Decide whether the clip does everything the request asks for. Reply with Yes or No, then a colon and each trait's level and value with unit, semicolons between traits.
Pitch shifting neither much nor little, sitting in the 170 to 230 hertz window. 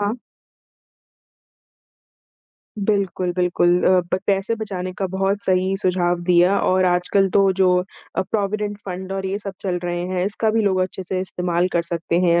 No: narrow, 1.7 semitones; medium, 185 Hz